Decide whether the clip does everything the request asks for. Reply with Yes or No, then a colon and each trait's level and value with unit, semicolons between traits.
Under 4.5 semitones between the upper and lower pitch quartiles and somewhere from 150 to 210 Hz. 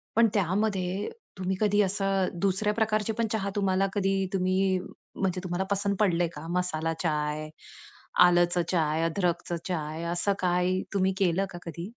Yes: narrow, 2.5 semitones; medium, 185 Hz